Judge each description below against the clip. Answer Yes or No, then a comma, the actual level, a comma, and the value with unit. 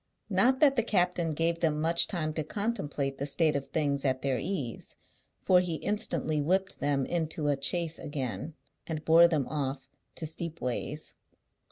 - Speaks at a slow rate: No, average, 165 wpm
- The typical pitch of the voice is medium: Yes, medium, 155 Hz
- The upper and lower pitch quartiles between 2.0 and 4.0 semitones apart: Yes, average, 3.4 semitones